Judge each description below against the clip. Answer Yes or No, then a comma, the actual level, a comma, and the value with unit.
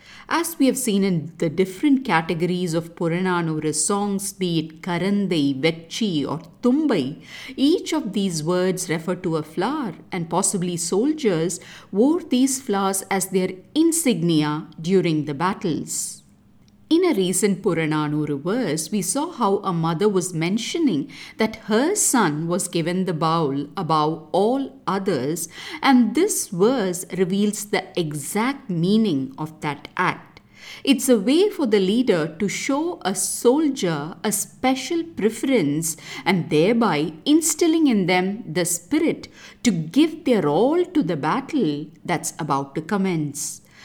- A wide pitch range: Yes, wide, 7.0 semitones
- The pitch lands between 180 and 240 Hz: Yes, high, 190 Hz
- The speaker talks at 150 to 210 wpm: No, slow, 135 wpm